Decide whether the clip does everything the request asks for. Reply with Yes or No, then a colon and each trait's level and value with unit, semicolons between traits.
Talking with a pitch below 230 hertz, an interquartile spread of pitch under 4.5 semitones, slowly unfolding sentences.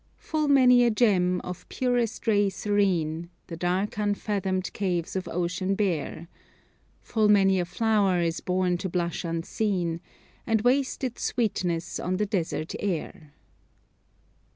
Yes: high, 190 Hz; average, 3.4 semitones; slow, 130 wpm